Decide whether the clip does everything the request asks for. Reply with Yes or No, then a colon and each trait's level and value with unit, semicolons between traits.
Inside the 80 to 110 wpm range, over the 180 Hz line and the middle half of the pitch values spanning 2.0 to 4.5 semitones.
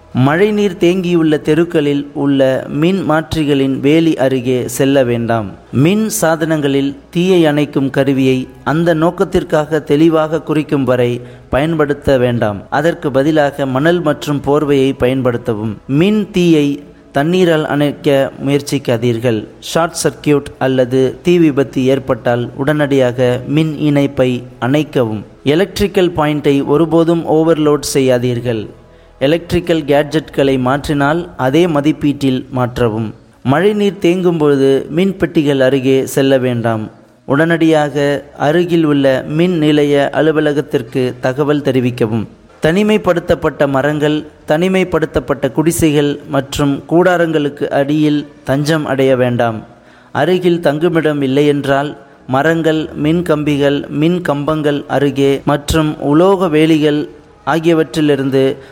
No: average, 95 wpm; medium, 145 Hz; average, 3.1 semitones